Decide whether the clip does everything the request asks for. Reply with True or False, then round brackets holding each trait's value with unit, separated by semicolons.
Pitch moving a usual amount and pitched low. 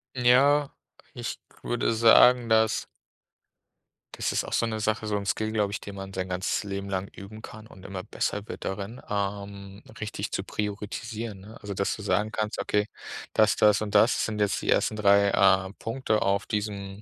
False (1.8 semitones; 105 Hz)